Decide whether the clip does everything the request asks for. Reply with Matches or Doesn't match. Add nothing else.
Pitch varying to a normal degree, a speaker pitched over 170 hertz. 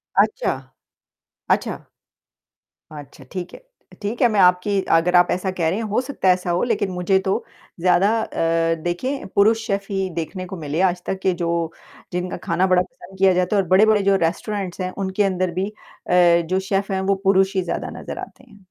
Doesn't match